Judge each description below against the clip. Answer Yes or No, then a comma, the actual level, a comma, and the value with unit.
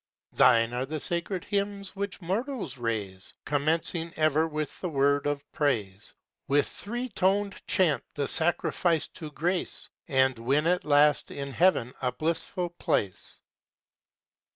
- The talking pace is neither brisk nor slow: No, slow, 130 wpm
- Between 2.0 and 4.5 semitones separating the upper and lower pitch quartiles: No, average, 4.9 semitones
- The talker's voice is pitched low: No, medium, 155 Hz